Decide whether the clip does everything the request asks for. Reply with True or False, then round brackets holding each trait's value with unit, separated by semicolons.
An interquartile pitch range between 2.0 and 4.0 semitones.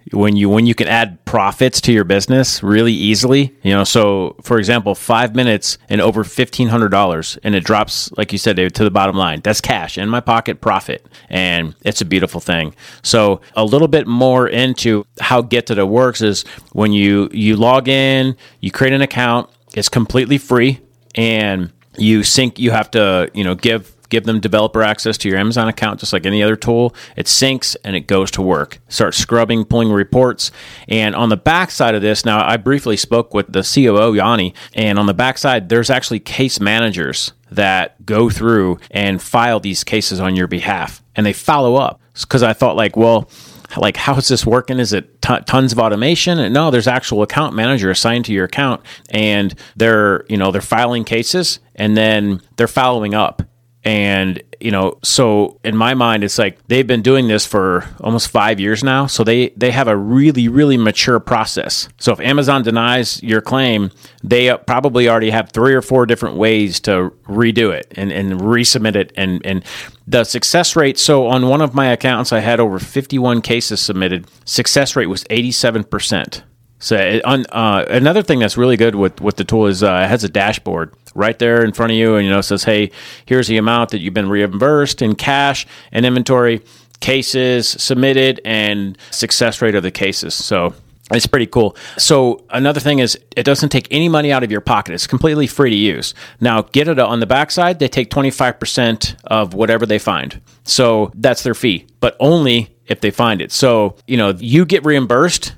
True (3.4 semitones)